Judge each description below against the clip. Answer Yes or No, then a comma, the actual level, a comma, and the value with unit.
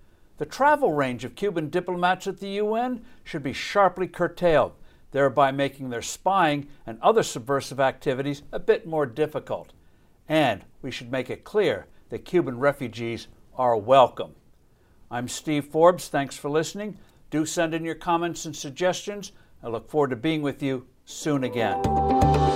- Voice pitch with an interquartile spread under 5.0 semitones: No, wide, 5.6 semitones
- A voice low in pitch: No, medium, 145 Hz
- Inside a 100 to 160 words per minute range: Yes, average, 155 wpm